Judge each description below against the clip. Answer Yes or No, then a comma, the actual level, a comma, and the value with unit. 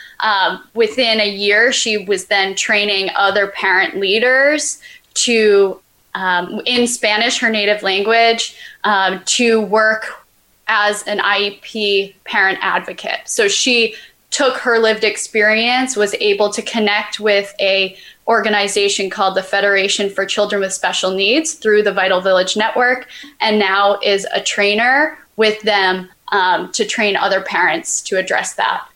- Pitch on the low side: No, high, 210 Hz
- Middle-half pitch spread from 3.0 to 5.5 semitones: No, narrow, 2.5 semitones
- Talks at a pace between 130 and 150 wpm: Yes, average, 140 wpm